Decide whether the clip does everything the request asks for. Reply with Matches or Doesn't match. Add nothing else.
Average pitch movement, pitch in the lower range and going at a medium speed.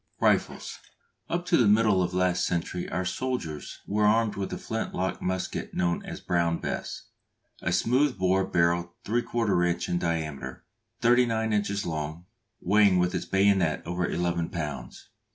Matches